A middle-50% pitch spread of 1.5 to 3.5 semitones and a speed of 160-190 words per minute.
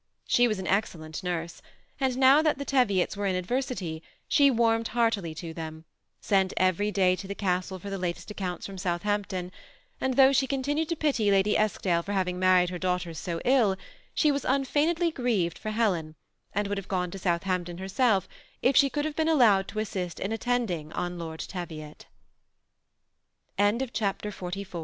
No: wide, 5.6 semitones; average, 165 wpm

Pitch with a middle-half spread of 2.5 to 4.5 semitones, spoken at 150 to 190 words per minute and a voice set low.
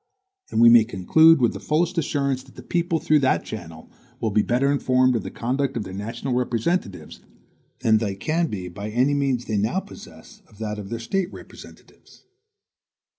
No: average, 5.2 semitones; average, 185 wpm; low, 125 Hz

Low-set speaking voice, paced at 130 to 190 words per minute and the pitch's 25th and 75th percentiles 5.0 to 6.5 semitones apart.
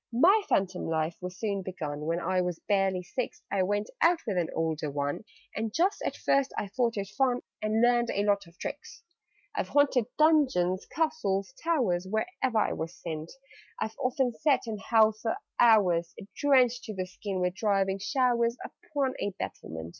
No: high, 205 Hz; average, 175 wpm; wide, 5.5 semitones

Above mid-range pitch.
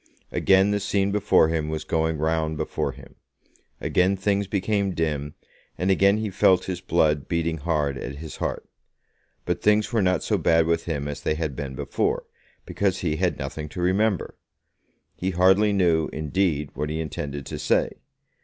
No: very low, 85 Hz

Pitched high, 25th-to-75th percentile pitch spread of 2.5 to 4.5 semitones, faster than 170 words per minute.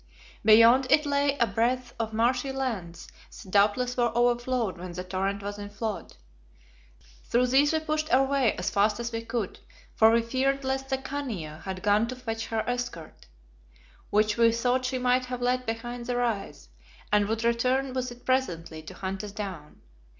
Yes: high, 235 Hz; average, 3.8 semitones; average, 180 wpm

